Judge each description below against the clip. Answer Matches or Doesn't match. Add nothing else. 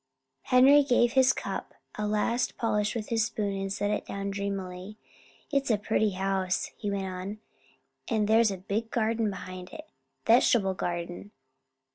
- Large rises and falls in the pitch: Doesn't match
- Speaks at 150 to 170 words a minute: Matches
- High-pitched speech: Matches